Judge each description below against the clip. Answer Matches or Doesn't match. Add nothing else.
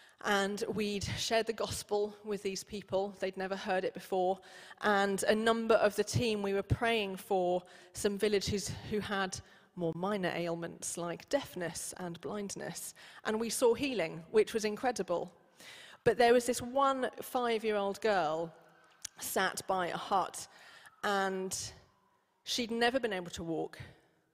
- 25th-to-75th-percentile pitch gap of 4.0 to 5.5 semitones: Doesn't match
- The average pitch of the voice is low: Doesn't match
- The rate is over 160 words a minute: Doesn't match